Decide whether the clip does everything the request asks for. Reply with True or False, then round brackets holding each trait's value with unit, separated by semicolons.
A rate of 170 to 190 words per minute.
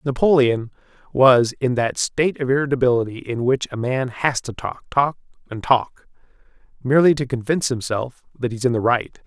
True (175 wpm)